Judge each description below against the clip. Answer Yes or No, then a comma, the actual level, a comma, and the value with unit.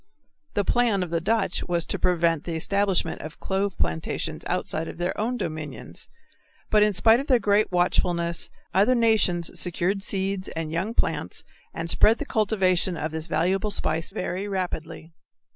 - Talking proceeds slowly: No, average, 160 wpm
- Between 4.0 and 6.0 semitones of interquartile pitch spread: No, average, 3.5 semitones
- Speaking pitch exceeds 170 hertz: Yes, medium, 185 Hz